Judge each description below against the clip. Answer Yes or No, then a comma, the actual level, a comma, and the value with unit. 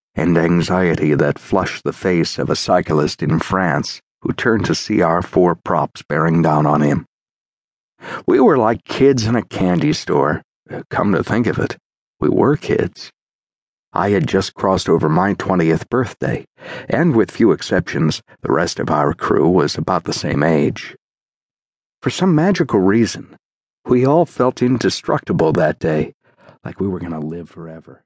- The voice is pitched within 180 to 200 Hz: No, very low, 95 Hz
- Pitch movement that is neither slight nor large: No, wide, 7.3 semitones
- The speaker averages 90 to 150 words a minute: No, average, 165 wpm